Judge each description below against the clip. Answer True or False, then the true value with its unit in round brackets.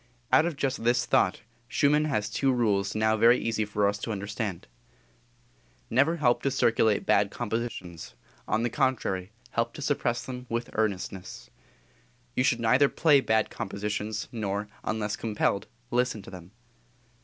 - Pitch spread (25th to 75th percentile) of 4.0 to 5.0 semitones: False (3.4 semitones)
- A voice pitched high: False (115 Hz)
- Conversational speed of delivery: True (150 wpm)